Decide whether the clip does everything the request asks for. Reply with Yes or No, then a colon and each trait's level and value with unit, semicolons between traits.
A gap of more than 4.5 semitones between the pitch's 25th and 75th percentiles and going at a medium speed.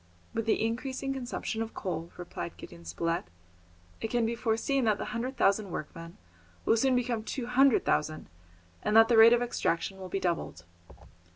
Yes: average, 5.2 semitones; average, 175 wpm